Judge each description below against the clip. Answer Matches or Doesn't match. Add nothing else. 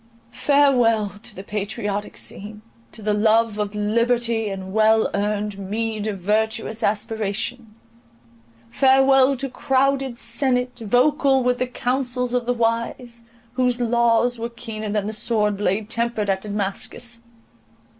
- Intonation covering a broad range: Doesn't match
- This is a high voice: Matches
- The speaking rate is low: Matches